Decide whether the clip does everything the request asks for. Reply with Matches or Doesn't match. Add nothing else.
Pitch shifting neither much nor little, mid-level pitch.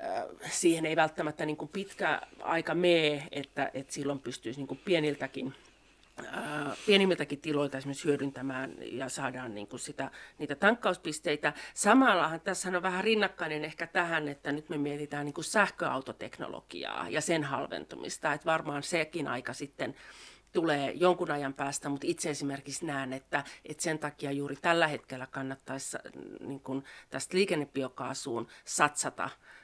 Matches